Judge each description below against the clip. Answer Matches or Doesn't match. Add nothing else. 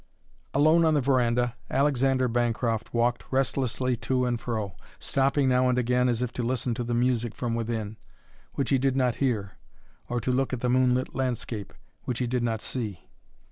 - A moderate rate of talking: Matches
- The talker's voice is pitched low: Matches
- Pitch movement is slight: Matches